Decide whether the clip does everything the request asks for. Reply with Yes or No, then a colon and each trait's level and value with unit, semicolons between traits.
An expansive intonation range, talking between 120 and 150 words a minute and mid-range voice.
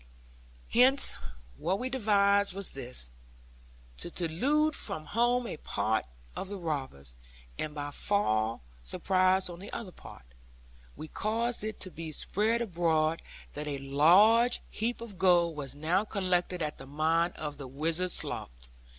Yes: wide, 5.7 semitones; average, 145 wpm; medium, 175 Hz